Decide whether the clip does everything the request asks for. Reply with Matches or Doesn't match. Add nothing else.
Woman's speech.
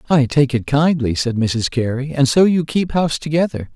Doesn't match